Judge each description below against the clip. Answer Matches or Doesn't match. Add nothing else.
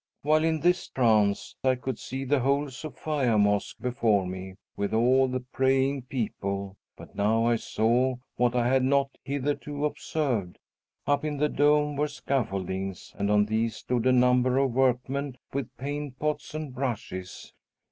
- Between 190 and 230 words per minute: Doesn't match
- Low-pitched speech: Matches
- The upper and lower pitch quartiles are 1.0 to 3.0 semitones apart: Doesn't match